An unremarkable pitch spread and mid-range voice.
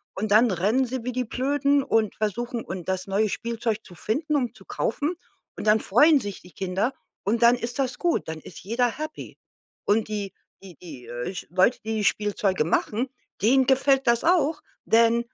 No: average, 4.5 semitones; high, 230 Hz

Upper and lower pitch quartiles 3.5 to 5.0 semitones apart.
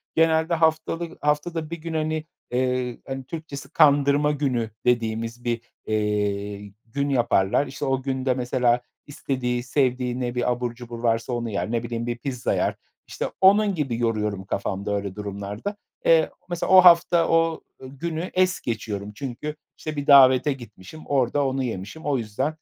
Yes: average, 4.7 semitones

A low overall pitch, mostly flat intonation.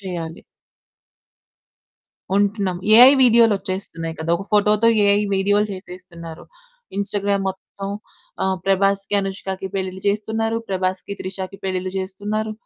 No: high, 195 Hz; narrow, 1.7 semitones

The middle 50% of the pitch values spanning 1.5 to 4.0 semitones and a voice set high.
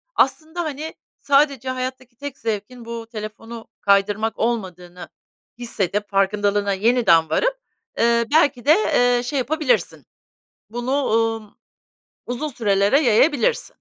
No: average, 4.5 semitones; high, 235 Hz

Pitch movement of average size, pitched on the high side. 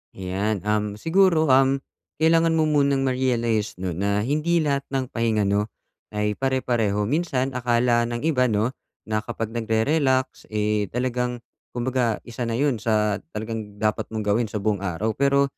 No: average, 4.1 semitones; low, 120 Hz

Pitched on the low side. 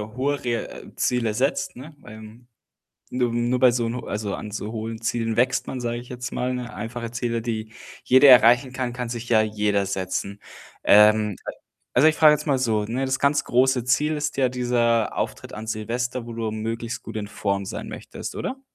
Yes: low, 120 Hz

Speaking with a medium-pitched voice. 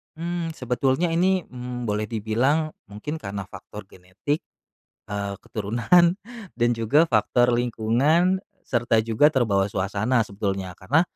No: low, 120 Hz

